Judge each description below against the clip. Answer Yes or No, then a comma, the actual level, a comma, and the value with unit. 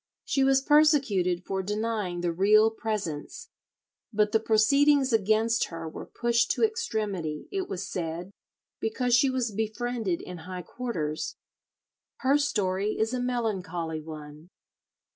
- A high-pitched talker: Yes, high, 215 Hz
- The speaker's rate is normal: No, slow, 130 wpm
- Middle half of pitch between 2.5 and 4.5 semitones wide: No, wide, 5.5 semitones